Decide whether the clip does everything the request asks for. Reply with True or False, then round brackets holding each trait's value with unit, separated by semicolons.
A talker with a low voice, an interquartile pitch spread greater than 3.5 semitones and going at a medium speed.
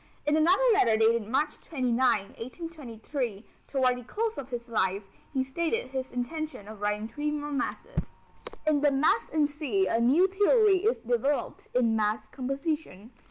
False (265 Hz; 5.2 semitones; 160 wpm)